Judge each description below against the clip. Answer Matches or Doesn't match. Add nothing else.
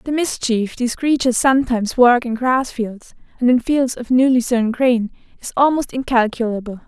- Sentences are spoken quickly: Doesn't match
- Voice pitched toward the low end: Doesn't match